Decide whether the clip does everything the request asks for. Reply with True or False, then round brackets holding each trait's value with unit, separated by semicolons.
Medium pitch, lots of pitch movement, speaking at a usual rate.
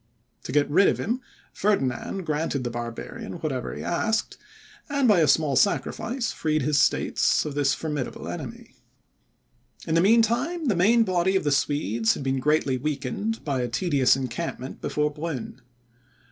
True (150 Hz; 6.6 semitones; 160 wpm)